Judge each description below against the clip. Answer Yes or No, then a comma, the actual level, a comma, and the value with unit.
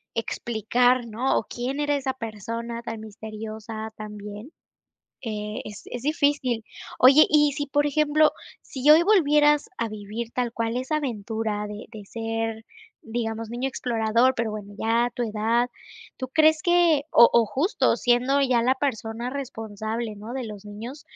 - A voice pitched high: Yes, high, 235 Hz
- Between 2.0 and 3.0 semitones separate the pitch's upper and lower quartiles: No, average, 3.7 semitones